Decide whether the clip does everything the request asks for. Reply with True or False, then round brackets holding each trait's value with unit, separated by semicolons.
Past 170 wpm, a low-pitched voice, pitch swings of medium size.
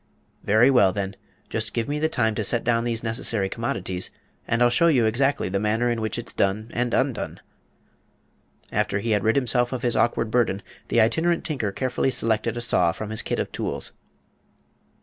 False (190 wpm; 115 Hz; 2.3 semitones)